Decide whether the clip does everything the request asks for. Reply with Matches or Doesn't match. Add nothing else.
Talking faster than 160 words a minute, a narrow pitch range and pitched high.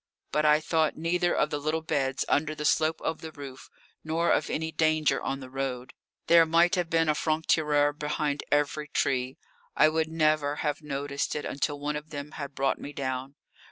Doesn't match